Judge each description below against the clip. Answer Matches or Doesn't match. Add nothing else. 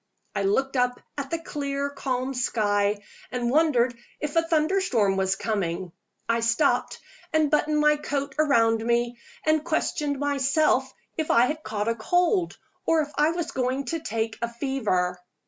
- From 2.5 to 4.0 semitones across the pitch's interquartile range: Doesn't match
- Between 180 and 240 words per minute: Doesn't match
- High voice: Matches